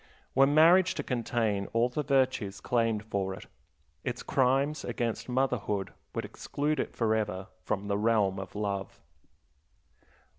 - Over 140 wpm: No, slow, 135 wpm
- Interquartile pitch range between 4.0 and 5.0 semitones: Yes, average, 4.7 semitones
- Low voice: Yes, low, 115 Hz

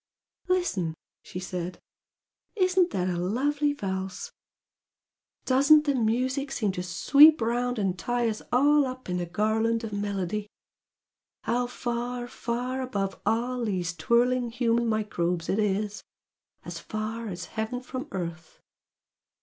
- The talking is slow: Yes, slow, 130 wpm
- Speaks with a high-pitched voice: Yes, high, 230 Hz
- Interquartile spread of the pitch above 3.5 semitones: Yes, average, 4.8 semitones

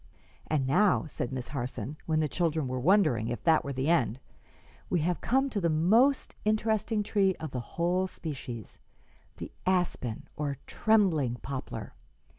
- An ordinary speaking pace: Yes, average, 155 wpm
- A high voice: No, medium, 160 Hz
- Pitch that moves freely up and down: Yes, wide, 6.5 semitones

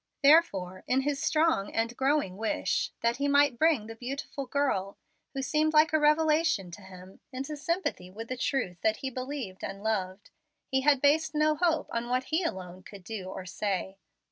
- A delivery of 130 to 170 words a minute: No, average, 185 wpm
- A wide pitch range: Yes, wide, 7.2 semitones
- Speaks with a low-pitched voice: No, very high, 255 Hz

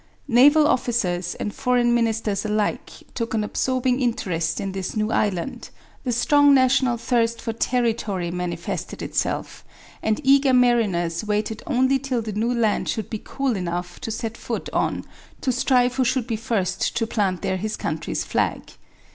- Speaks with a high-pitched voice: Yes, high, 230 Hz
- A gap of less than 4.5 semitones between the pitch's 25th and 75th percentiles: Yes, average, 3.5 semitones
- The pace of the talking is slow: No, average, 160 wpm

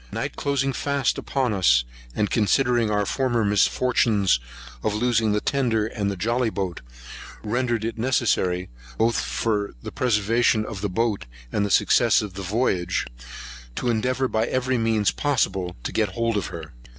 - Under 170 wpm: Yes, average, 155 wpm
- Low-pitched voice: Yes, low, 110 Hz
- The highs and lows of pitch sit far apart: No, average, 3.2 semitones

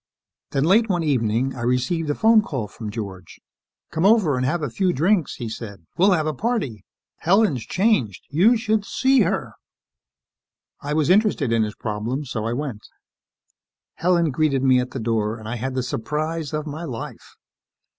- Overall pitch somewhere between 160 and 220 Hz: No, medium, 145 Hz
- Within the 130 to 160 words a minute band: No, average, 175 wpm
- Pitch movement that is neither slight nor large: No, wide, 7.2 semitones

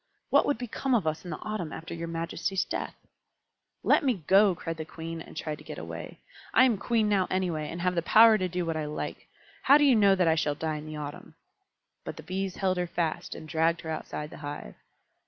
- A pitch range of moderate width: Yes, average, 3.8 semitones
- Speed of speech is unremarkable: No, fast, 235 wpm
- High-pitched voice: No, medium, 170 Hz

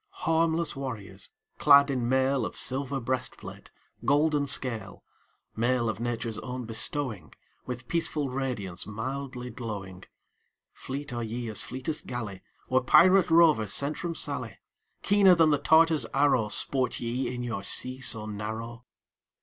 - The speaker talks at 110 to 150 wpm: Yes, slow, 135 wpm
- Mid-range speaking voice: No, low, 125 Hz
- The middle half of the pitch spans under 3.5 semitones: No, average, 3.9 semitones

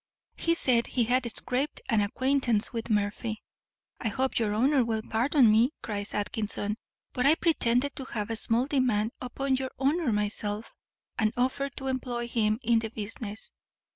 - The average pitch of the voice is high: Yes, high, 235 Hz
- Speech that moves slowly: No, average, 165 wpm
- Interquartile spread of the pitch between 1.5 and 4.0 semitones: Yes, average, 3.3 semitones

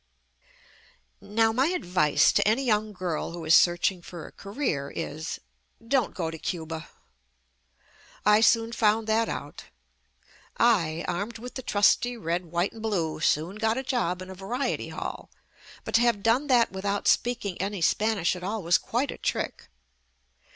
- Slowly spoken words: No, average, 165 wpm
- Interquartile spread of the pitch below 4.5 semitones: No, average, 4.8 semitones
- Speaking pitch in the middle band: No, high, 205 Hz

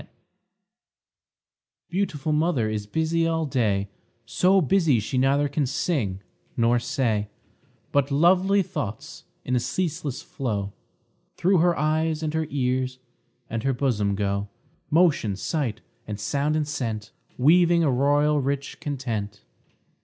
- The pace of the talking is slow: Yes, slow, 130 wpm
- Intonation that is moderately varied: No, wide, 5.8 semitones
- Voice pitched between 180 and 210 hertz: No, medium, 140 Hz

